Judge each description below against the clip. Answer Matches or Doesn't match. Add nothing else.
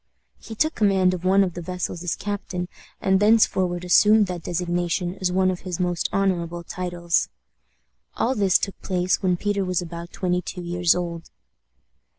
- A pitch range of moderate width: Doesn't match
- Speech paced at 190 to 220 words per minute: Doesn't match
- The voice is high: Doesn't match